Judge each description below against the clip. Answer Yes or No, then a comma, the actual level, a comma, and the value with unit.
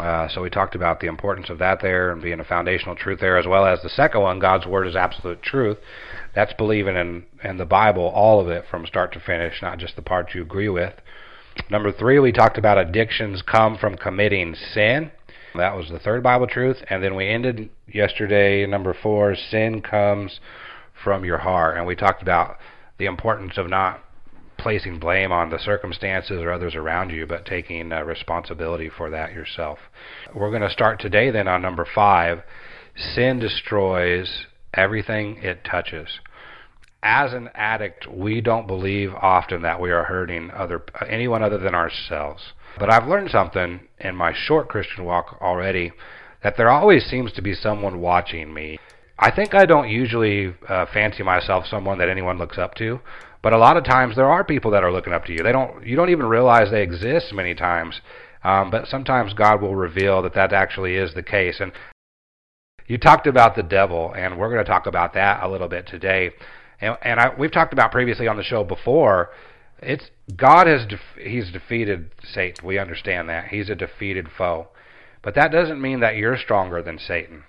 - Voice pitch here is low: Yes, very low, 95 Hz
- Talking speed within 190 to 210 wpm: Yes, average, 195 wpm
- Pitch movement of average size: Yes, average, 3.7 semitones